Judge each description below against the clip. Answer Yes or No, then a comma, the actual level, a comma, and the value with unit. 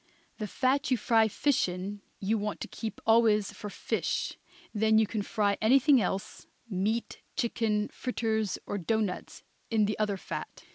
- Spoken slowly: No, average, 155 wpm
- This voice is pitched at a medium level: No, high, 215 Hz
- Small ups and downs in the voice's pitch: Yes, narrow, 1.9 semitones